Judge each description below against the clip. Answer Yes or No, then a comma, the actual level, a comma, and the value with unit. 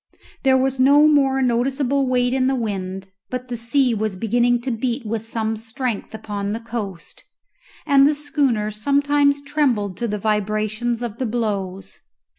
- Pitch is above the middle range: Yes, high, 240 Hz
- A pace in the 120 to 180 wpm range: Yes, average, 160 wpm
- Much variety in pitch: No, average, 3.9 semitones